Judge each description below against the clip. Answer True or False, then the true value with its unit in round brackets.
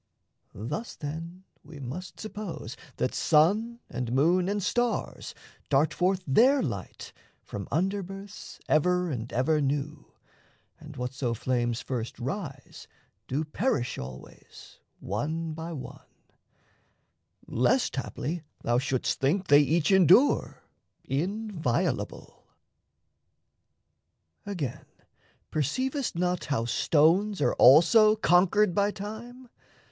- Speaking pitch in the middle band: True (160 Hz)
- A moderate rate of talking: False (105 wpm)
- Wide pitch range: True (6.6 semitones)